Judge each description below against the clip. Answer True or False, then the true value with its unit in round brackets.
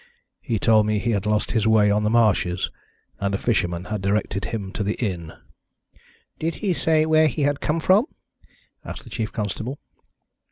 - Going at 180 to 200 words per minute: True (185 wpm)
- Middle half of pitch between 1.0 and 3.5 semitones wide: False (5.6 semitones)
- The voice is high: False (110 Hz)